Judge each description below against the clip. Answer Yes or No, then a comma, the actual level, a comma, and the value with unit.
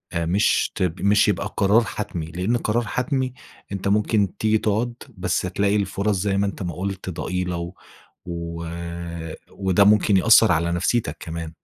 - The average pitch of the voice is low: Yes, low, 100 Hz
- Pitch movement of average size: Yes, average, 3.5 semitones